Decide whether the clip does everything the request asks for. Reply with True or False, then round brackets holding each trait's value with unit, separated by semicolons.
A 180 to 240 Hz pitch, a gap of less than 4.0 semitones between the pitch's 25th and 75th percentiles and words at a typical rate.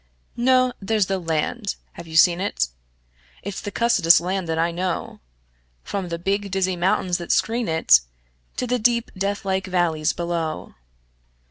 True (185 Hz; 3.0 semitones; 150 wpm)